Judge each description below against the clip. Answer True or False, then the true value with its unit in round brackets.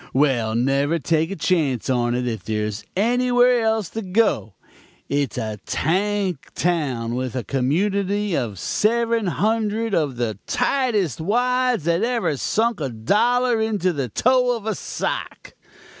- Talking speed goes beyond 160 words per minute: False (145 wpm)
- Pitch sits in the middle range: True (180 Hz)